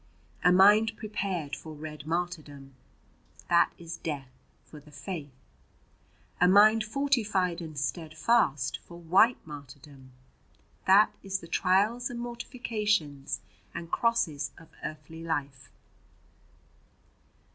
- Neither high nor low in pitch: Yes, medium, 170 Hz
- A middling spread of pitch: No, wide, 5.9 semitones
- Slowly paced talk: Yes, slow, 105 wpm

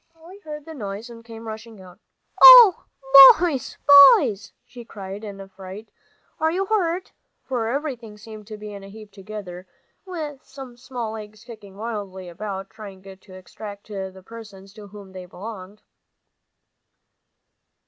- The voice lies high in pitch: Yes, high, 215 Hz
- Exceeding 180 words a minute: No, average, 150 wpm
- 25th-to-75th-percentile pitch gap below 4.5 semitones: Yes, average, 3.9 semitones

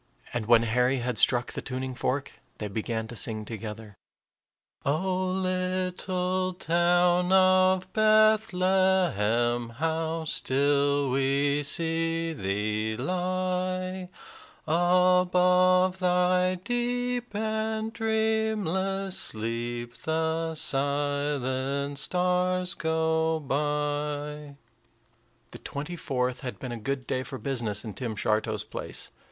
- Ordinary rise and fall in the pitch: No, wide, 6.1 semitones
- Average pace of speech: No, slow, 100 wpm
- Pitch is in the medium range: Yes, medium, 160 Hz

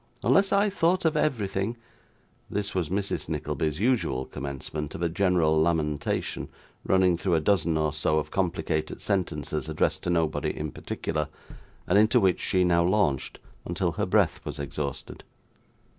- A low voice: Yes, very low, 85 Hz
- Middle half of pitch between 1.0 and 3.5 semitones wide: No, average, 4.5 semitones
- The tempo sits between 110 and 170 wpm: Yes, average, 155 wpm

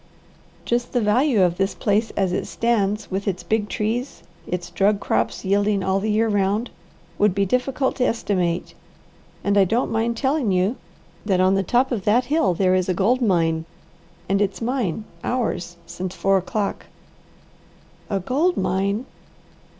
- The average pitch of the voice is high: Yes, high, 205 Hz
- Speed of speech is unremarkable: Yes, average, 165 wpm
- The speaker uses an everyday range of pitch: Yes, average, 3.8 semitones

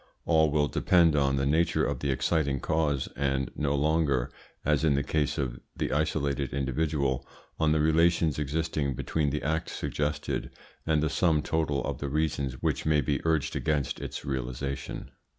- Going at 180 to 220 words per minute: No, average, 170 wpm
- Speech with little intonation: Yes, narrow, 2.3 semitones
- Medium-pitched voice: No, very low, 75 Hz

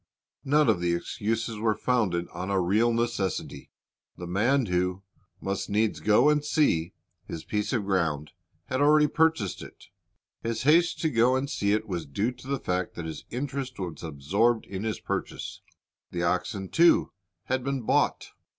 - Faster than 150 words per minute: Yes, average, 170 wpm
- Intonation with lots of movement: Yes, wide, 5.9 semitones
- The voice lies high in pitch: No, low, 110 Hz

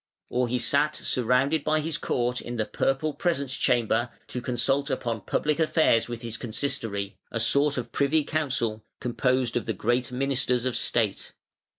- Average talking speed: Yes, average, 165 wpm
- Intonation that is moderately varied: Yes, average, 3.1 semitones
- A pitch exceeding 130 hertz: No, low, 125 Hz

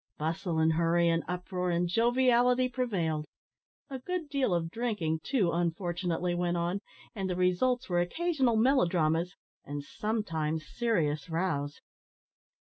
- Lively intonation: Yes, wide, 6.2 semitones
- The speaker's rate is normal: No, slow, 125 wpm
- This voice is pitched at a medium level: Yes, medium, 180 Hz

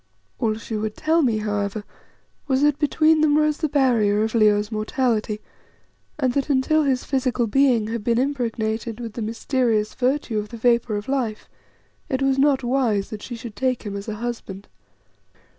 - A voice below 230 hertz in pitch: No, high, 235 Hz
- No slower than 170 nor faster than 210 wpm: Yes, average, 175 wpm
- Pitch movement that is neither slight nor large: Yes, average, 3.9 semitones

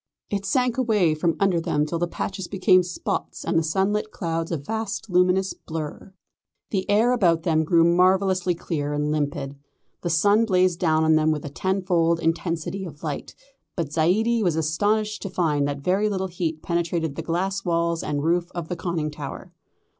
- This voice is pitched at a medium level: Yes, medium, 170 Hz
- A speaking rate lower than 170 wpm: No, average, 180 wpm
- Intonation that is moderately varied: Yes, average, 3.2 semitones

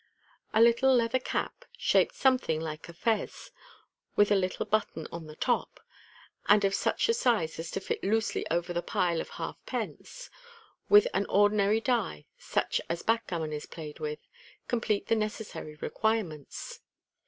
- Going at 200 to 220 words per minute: No, average, 155 wpm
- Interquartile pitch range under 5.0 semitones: No, wide, 5.6 semitones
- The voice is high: Yes, high, 205 Hz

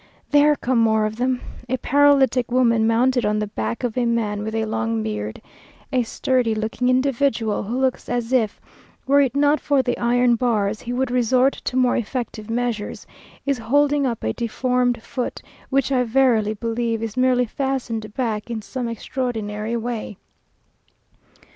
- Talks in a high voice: Yes, high, 240 Hz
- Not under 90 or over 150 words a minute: No, average, 165 wpm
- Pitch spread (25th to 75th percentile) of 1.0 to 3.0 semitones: Yes, average, 2.7 semitones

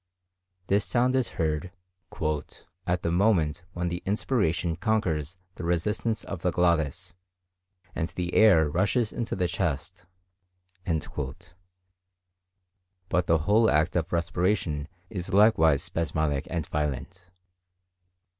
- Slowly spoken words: Yes, slow, 110 wpm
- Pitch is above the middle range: No, very low, 90 Hz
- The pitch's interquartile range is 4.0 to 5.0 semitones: No, average, 2.9 semitones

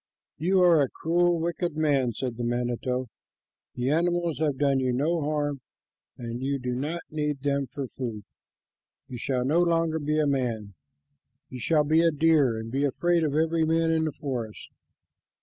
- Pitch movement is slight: No, average, 4.2 semitones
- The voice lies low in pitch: No, medium, 145 Hz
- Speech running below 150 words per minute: No, average, 175 wpm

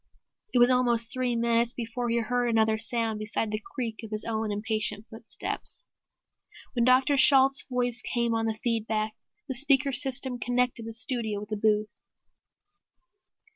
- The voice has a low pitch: No, high, 235 Hz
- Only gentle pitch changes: Yes, narrow, 2.1 semitones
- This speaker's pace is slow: No, average, 160 wpm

